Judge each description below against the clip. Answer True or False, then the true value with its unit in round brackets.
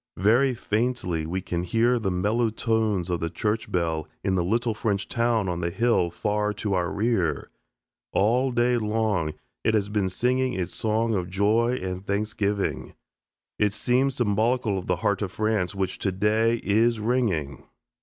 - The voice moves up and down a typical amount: True (3.7 semitones)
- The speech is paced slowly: False (165 wpm)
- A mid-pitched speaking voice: False (105 Hz)